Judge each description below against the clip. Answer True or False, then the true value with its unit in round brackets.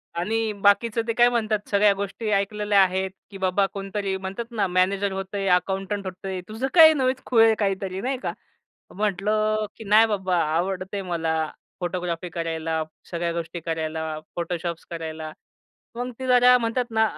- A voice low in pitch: False (195 Hz)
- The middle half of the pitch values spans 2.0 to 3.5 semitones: True (3.2 semitones)